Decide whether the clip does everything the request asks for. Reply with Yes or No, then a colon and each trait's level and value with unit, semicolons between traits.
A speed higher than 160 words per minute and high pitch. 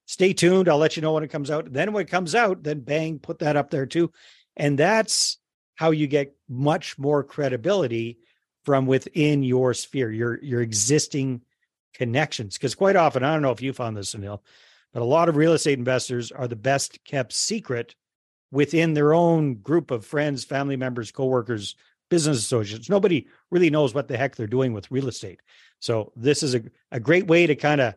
No: average, 200 wpm; medium, 140 Hz